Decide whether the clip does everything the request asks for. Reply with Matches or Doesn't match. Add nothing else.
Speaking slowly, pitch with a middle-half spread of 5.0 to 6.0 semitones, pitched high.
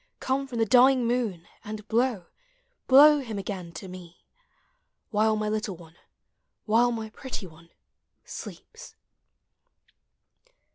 Doesn't match